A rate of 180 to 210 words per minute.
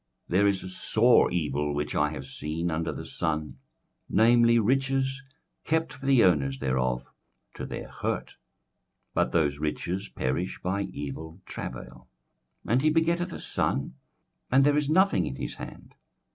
No: average, 160 wpm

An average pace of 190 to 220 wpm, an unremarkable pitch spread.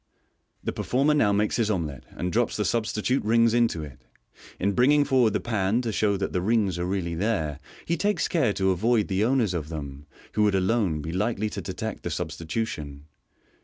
Yes: average, 195 wpm; average, 5.0 semitones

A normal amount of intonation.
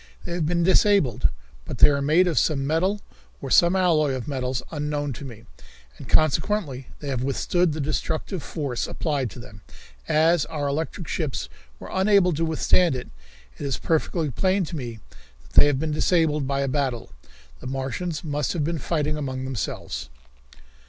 Yes: average, 4.0 semitones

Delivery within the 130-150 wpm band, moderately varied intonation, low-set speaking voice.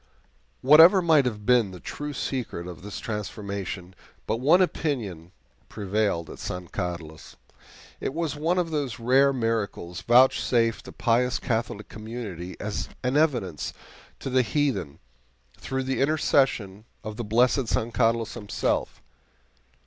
Yes: slow, 135 wpm; average, 4.9 semitones; low, 115 Hz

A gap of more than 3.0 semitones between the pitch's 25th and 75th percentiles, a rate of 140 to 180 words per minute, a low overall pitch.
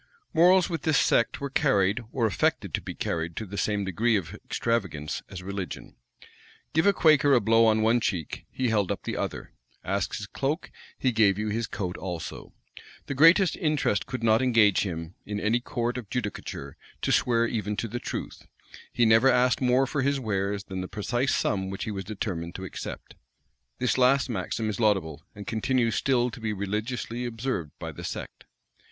No: average, 4.1 semitones; average, 190 wpm; low, 110 Hz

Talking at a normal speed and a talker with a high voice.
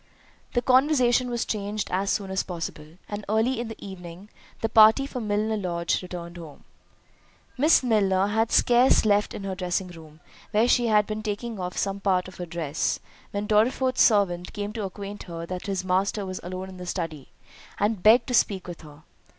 Yes: average, 185 wpm; high, 200 Hz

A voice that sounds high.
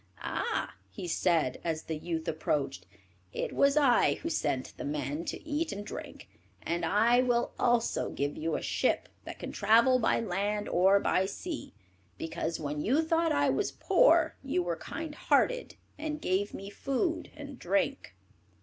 Yes: high, 205 Hz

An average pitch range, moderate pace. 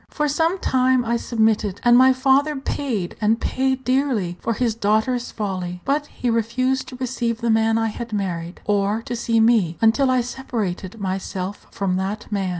Yes: average, 4.1 semitones; average, 175 wpm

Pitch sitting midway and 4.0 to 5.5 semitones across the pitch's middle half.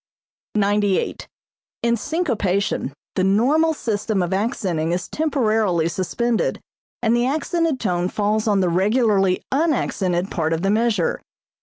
No: high, 210 Hz; average, 4.5 semitones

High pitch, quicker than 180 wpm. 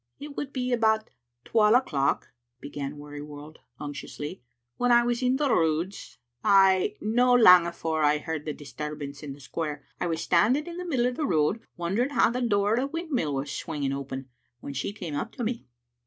No: medium, 180 Hz; average, 195 wpm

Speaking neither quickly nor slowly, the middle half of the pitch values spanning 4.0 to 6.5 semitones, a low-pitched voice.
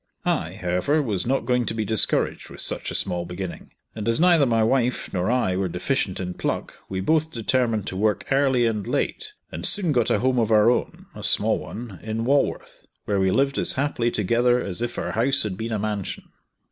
No: fast, 210 wpm; average, 4.5 semitones; low, 115 Hz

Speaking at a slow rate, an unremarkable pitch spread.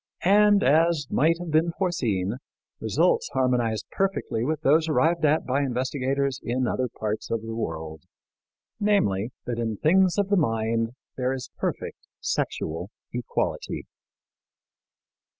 No: slow, 130 wpm; wide, 6.6 semitones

